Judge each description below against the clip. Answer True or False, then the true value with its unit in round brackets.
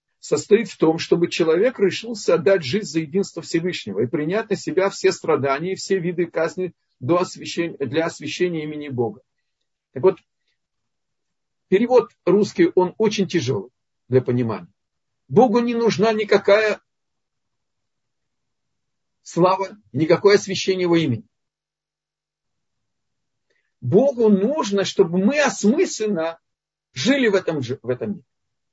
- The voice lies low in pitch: False (185 Hz)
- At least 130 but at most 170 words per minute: False (115 wpm)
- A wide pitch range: False (4.0 semitones)